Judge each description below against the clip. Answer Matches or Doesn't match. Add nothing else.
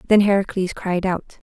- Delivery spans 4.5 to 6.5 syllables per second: Matches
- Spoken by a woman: Matches